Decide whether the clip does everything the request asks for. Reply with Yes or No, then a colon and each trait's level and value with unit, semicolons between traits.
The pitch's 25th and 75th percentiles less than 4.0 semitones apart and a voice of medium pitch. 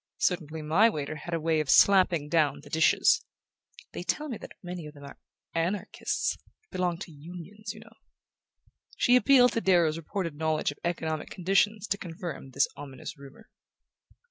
No: average, 4.3 semitones; medium, 170 Hz